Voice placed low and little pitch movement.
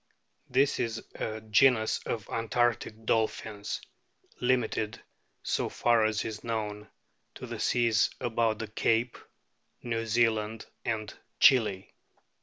Yes: low, 110 Hz; narrow, 1.5 semitones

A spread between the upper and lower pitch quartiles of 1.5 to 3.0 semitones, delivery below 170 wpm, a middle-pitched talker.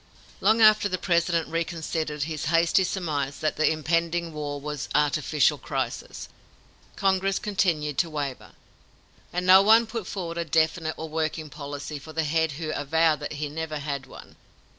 Yes: narrow, 2.5 semitones; average, 160 wpm; medium, 160 Hz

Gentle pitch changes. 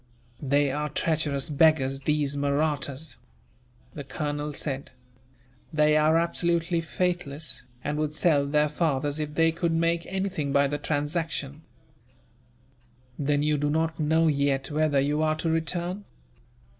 Yes: narrow, 2.2 semitones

